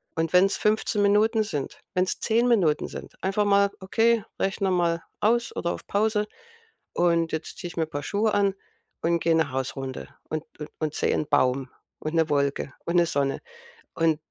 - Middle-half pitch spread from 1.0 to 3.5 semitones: No, average, 4.8 semitones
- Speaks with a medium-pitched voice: Yes, medium, 170 Hz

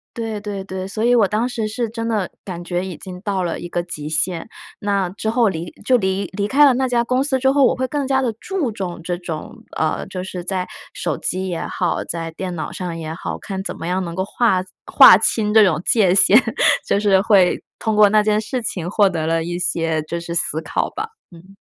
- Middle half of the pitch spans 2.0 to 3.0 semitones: No, average, 4.1 semitones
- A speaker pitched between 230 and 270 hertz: No, high, 190 Hz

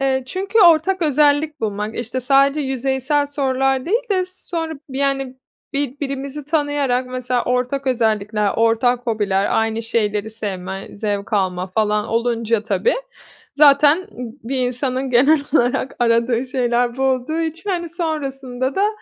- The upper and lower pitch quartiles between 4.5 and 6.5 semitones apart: No, average, 4.1 semitones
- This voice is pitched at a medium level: No, very high, 260 Hz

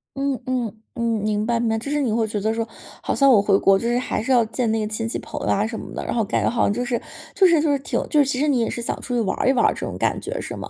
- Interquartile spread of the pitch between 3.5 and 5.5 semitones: No, average, 3.1 semitones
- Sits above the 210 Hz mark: Yes, high, 235 Hz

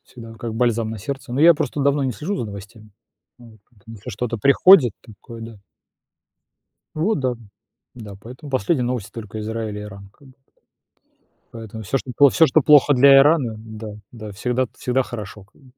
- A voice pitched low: Yes, low, 120 Hz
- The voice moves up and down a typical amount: Yes, average, 3.8 semitones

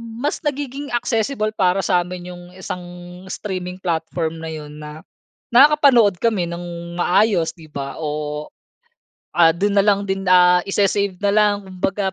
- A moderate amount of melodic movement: Yes, average, 3.4 semitones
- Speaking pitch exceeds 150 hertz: Yes, medium, 185 Hz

